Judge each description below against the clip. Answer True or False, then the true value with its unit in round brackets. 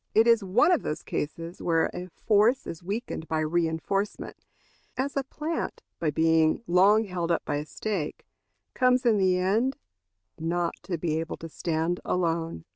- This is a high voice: False (175 Hz)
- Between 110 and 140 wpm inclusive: False (165 wpm)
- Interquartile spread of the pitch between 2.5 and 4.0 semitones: False (4.9 semitones)